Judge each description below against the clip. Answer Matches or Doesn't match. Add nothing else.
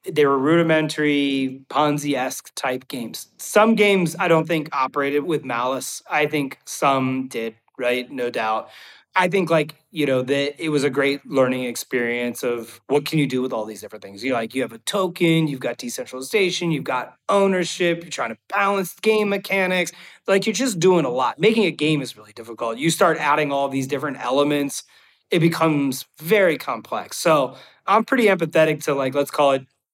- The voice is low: Doesn't match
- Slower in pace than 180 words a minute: Doesn't match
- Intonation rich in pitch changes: Doesn't match